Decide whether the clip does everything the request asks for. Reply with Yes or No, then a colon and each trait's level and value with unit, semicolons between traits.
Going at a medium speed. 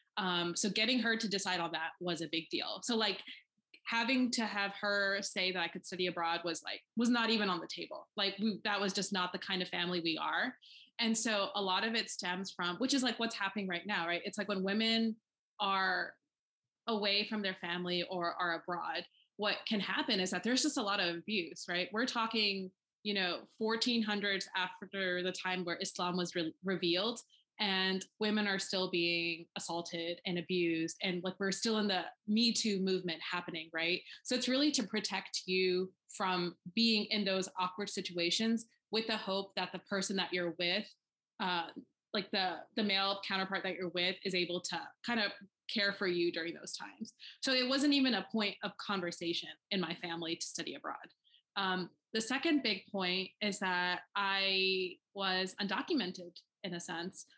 Yes: average, 190 wpm